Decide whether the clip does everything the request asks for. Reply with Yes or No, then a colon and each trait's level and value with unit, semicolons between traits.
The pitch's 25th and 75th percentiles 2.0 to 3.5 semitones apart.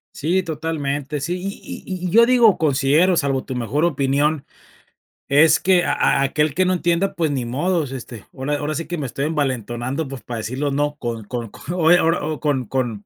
No: average, 3.9 semitones